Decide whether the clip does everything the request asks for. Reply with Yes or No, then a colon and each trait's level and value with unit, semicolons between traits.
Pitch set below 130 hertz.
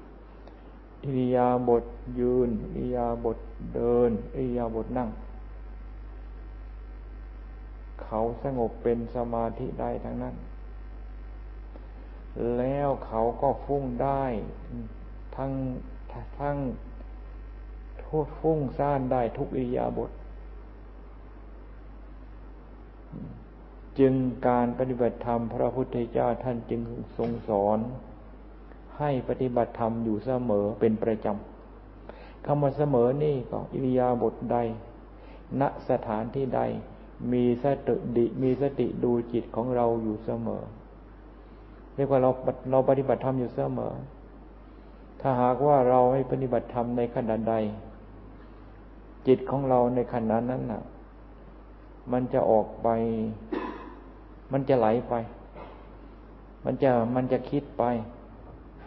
Yes: low, 120 Hz